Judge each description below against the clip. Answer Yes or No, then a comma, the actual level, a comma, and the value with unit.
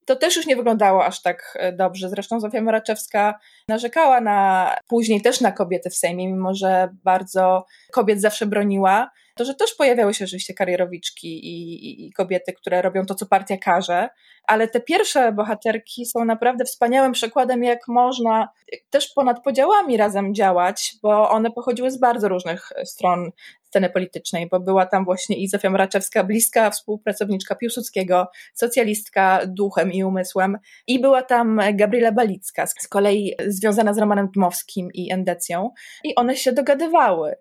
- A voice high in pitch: Yes, high, 210 Hz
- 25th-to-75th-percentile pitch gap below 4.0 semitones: No, average, 4.3 semitones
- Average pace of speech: Yes, average, 150 wpm